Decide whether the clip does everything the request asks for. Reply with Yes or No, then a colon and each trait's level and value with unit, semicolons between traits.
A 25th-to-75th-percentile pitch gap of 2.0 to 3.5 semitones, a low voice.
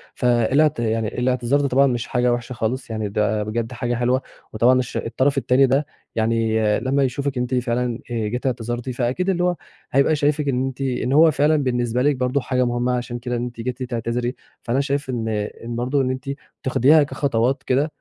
Yes: narrow, 2.4 semitones; low, 125 Hz